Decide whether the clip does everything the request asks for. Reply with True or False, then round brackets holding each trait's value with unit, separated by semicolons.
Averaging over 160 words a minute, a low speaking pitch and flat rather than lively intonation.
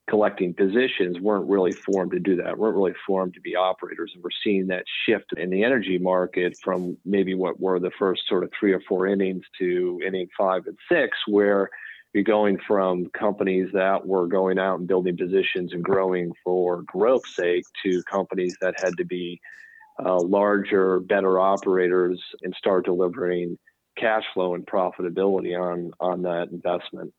True (170 wpm; 95 Hz; 1.5 semitones)